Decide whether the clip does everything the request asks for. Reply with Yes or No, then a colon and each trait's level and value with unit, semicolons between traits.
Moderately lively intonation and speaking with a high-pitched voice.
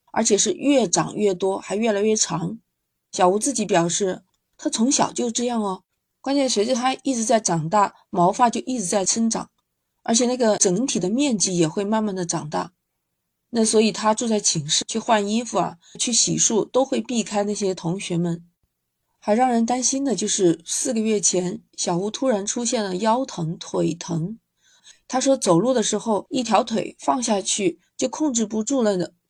Yes: average, 4.6 semitones; high, 210 Hz